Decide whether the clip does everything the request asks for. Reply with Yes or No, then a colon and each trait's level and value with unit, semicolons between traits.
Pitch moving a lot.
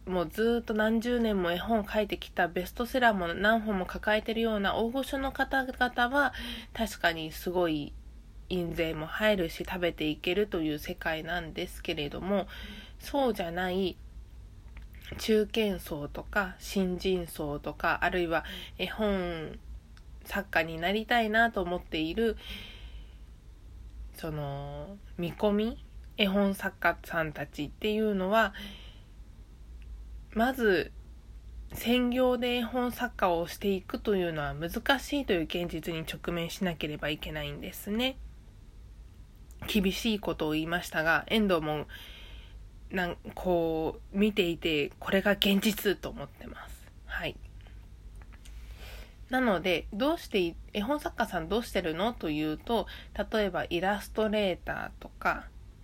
Yes: wide, 5.7 semitones